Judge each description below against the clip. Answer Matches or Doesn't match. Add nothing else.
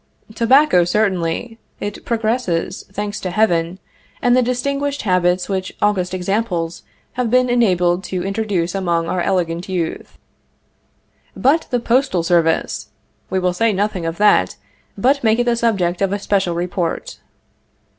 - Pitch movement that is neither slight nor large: Matches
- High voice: Matches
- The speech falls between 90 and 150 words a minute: Matches